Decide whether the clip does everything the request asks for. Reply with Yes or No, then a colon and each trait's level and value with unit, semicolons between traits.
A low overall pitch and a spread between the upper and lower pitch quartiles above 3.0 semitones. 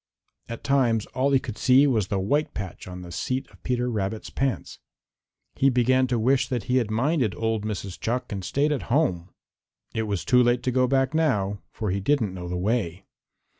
Yes: low, 120 Hz; average, 4.5 semitones